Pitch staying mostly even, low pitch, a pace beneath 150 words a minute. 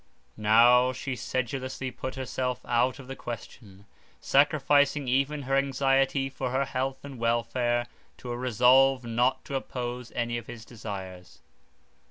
Yes: narrow, 2.1 semitones; low, 125 Hz; average, 140 wpm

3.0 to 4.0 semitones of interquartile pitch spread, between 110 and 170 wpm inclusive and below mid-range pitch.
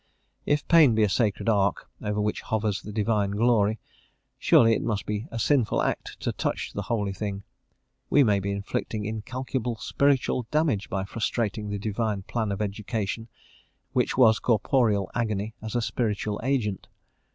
No: narrow, 2.5 semitones; average, 160 wpm; low, 110 Hz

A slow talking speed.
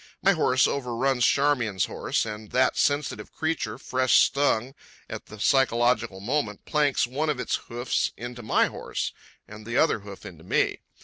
No: average, 160 wpm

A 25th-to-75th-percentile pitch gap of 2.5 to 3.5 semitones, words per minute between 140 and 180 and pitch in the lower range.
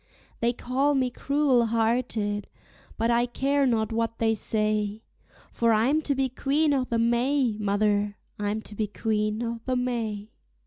No: average, 3.1 semitones; average, 160 wpm; high, 230 Hz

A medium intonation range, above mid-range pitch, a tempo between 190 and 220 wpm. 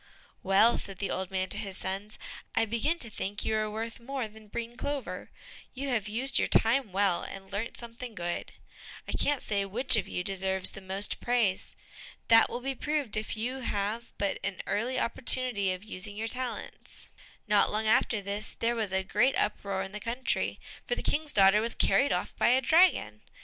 Yes: average, 3.8 semitones; high, 220 Hz; average, 195 wpm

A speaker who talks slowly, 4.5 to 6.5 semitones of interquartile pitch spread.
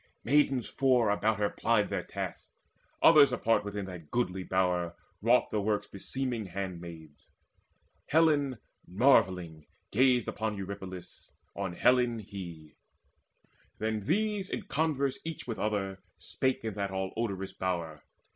Yes: slow, 125 wpm; average, 5.1 semitones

